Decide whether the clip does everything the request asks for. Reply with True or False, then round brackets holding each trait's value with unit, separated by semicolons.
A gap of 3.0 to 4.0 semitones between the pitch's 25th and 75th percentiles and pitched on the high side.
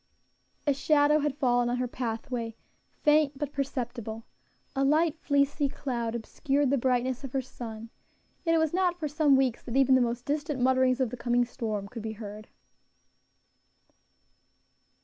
True (3.4 semitones; 260 Hz)